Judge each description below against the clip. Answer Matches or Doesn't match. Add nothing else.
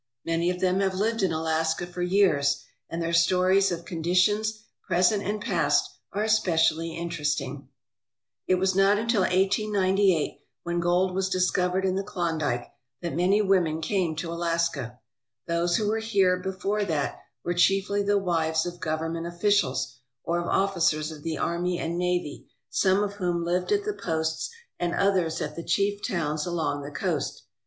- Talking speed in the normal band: Matches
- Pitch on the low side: Doesn't match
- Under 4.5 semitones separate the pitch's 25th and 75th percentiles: Matches